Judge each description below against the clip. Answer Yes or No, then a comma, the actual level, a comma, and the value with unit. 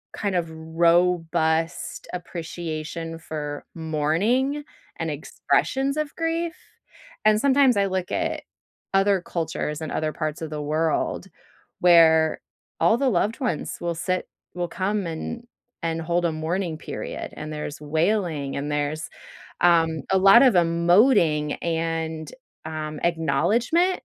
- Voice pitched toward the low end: No, medium, 170 Hz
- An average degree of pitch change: Yes, average, 3.8 semitones